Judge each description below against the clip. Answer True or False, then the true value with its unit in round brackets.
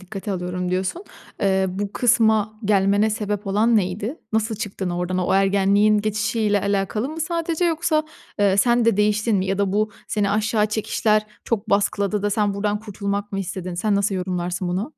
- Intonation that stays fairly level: True (1.9 semitones)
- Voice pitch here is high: True (205 Hz)